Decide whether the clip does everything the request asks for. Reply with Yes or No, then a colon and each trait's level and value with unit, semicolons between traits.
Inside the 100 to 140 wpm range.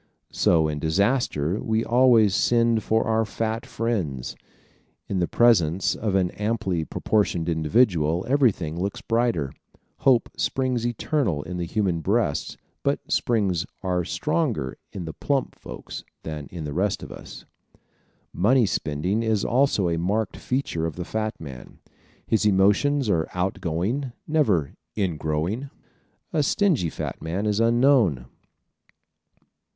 Yes: slow, 135 wpm